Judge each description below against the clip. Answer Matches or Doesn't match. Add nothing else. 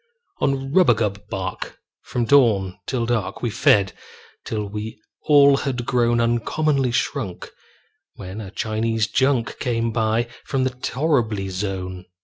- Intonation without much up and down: Doesn't match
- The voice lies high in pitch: Doesn't match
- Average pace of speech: Doesn't match